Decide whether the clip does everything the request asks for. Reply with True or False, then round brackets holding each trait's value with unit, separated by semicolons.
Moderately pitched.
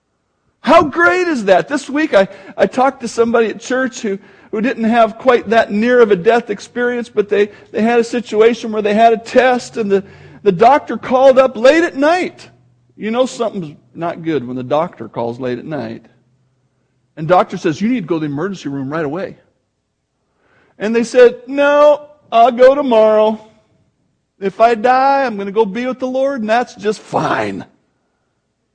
False (230 Hz)